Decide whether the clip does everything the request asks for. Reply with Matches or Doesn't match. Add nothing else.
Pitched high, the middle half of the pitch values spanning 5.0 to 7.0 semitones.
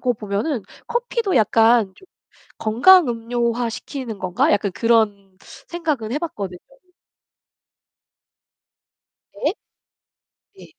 Matches